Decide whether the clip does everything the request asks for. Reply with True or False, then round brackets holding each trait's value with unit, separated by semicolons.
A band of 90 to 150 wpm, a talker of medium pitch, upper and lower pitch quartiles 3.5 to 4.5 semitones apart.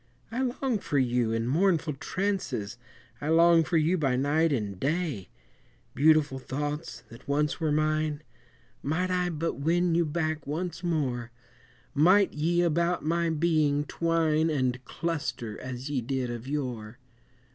True (145 wpm; 155 Hz; 4.2 semitones)